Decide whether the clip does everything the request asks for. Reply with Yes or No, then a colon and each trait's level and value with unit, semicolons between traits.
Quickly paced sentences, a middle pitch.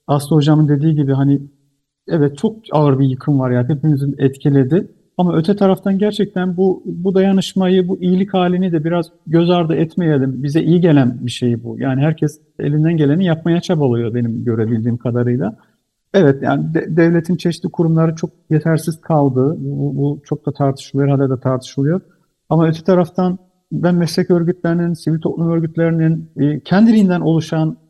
Yes: fast, 155 wpm; medium, 160 Hz